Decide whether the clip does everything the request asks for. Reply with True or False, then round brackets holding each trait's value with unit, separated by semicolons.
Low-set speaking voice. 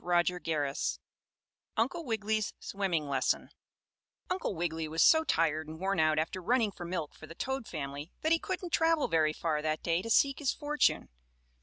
False (175 Hz)